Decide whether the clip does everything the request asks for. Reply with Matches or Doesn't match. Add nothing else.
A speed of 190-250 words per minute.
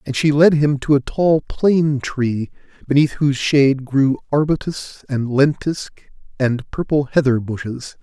Doesn't match